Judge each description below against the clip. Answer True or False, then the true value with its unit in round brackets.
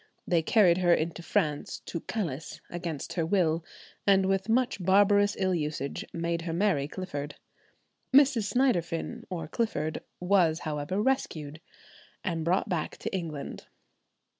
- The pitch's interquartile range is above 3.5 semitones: True (4.0 semitones)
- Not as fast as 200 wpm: True (135 wpm)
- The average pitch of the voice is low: False (175 Hz)